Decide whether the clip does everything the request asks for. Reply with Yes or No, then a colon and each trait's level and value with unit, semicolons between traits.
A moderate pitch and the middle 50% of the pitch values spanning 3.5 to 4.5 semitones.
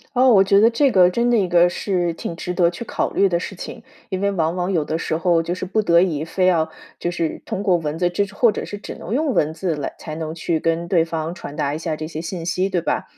No: medium, 175 Hz; average, 2.9 semitones